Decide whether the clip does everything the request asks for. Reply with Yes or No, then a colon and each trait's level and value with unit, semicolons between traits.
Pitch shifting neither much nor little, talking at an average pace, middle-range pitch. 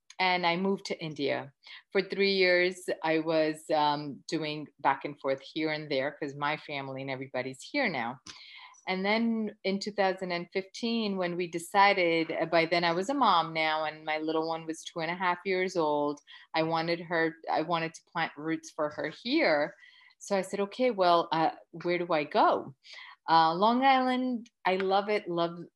Yes: average, 3.8 semitones; average, 180 wpm; medium, 170 Hz